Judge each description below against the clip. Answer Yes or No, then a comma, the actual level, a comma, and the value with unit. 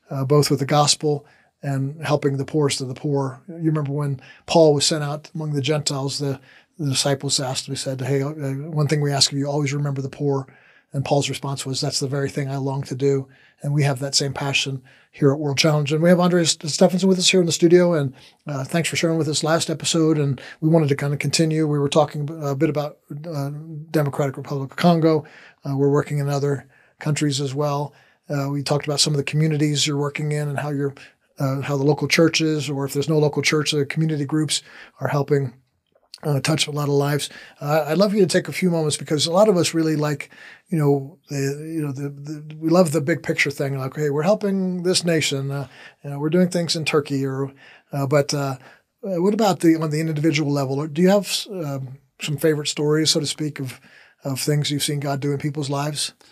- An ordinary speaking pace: No, fast, 235 wpm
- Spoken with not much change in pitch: Yes, narrow, 2.1 semitones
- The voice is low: No, medium, 145 Hz